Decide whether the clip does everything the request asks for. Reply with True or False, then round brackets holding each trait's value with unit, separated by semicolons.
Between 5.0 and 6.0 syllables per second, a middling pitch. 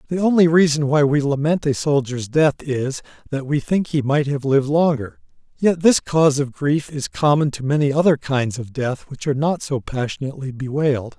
True (5.3 syllables/s; 145 Hz)